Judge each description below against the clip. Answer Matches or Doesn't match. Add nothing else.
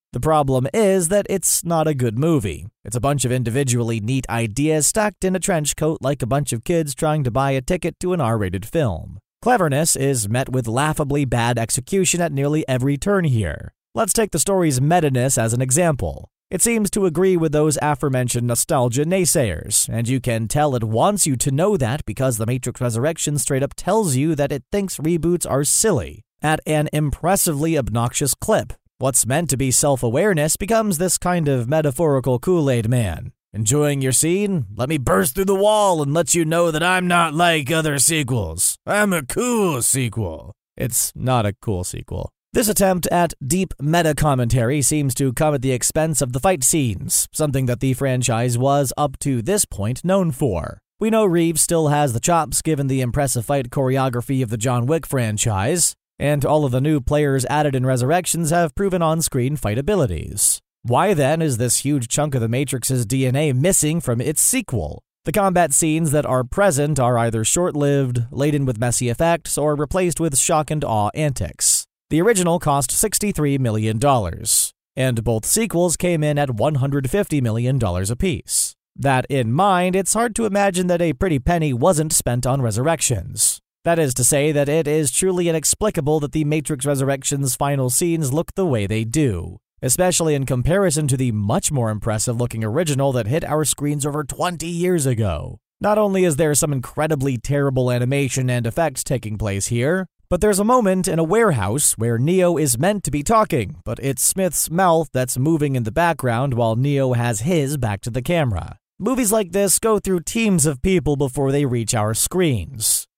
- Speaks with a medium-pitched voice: Matches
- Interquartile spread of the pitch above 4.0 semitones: Matches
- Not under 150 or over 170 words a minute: Doesn't match